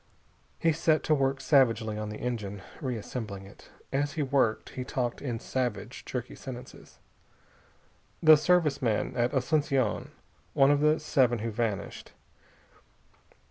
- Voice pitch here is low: Yes, low, 130 Hz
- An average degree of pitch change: Yes, average, 4.0 semitones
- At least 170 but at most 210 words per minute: No, slow, 135 wpm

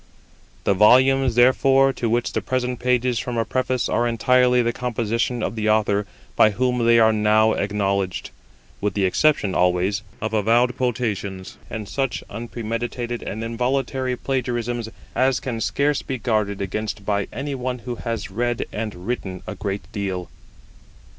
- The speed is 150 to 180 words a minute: Yes, average, 155 wpm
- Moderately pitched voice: No, low, 115 Hz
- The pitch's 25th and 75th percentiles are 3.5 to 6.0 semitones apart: No, average, 3.1 semitones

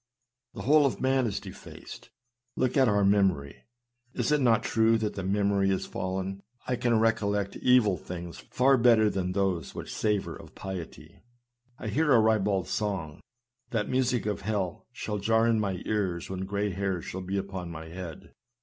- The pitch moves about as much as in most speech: Yes, average, 3.1 semitones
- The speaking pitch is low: Yes, low, 100 Hz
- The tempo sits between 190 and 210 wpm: No, average, 175 wpm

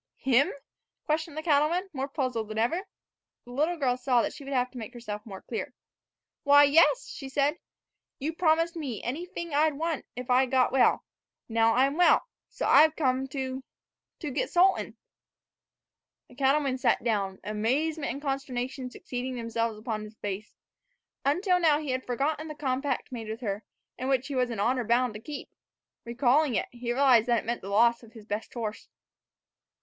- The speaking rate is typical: Yes, average, 180 wpm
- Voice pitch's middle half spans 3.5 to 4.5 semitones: Yes, average, 3.9 semitones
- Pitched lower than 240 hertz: No, very high, 260 Hz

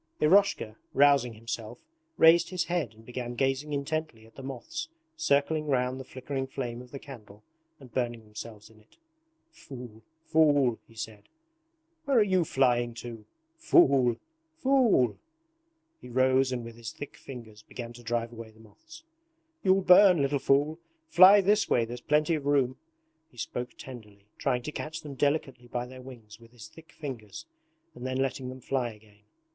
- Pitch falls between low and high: No, low, 130 Hz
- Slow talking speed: No, average, 165 wpm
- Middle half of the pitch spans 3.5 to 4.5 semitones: Yes, average, 4.2 semitones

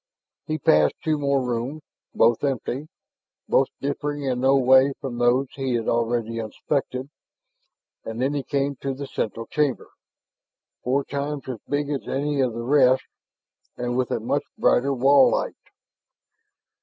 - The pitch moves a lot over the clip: No, narrow, 2.5 semitones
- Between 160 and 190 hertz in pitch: No, low, 135 Hz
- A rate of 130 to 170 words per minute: Yes, average, 150 wpm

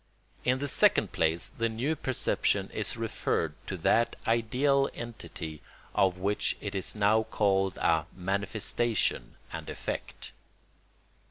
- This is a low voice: Yes, low, 105 Hz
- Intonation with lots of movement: No, average, 3.8 semitones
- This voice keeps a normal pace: No, slow, 120 wpm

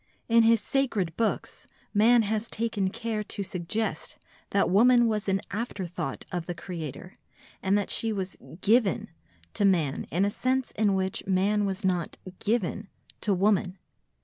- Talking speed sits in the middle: Yes, average, 150 wpm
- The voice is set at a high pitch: Yes, high, 200 Hz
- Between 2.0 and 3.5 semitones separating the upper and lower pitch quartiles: Yes, average, 3.2 semitones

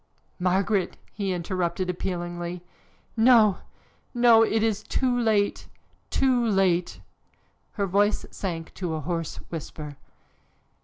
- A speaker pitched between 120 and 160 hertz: No, high, 190 Hz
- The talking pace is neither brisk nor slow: No, slow, 105 wpm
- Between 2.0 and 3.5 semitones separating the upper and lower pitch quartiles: No, average, 4.1 semitones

